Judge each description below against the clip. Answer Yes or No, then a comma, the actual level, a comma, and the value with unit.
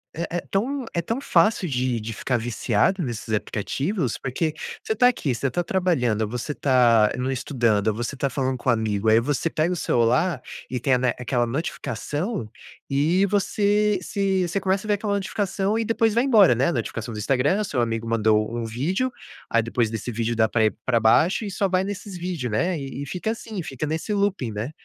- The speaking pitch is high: No, medium, 140 Hz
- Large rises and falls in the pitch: Yes, wide, 8.5 semitones